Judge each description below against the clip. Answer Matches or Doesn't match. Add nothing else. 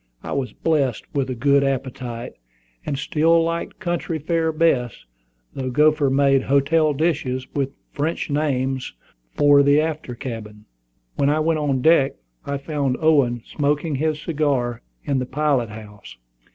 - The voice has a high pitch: Doesn't match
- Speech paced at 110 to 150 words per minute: Matches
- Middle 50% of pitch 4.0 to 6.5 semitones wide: Doesn't match